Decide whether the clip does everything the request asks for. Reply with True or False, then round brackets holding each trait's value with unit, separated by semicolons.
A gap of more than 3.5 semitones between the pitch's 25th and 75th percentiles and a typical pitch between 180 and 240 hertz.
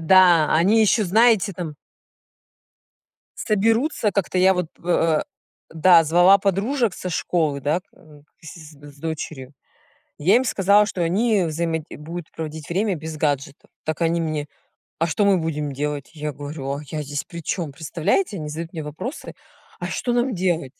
False (4.2 semitones; 165 Hz)